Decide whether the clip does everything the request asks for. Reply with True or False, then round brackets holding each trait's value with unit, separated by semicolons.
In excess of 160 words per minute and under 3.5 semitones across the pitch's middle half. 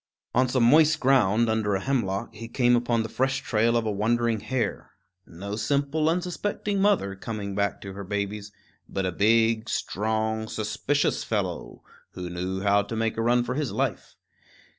False (170 wpm; 3.8 semitones)